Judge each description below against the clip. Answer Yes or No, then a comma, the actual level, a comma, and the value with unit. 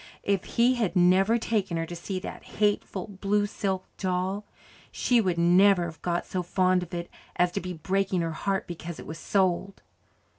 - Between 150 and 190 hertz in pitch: Yes, medium, 185 Hz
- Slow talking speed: No, average, 185 wpm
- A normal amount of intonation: No, narrow, 2.3 semitones